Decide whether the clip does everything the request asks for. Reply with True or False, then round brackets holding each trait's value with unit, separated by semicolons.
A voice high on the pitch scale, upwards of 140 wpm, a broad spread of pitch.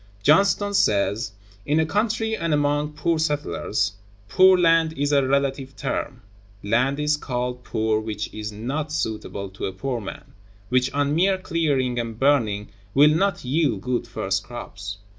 False (140 Hz; 155 wpm; 6.1 semitones)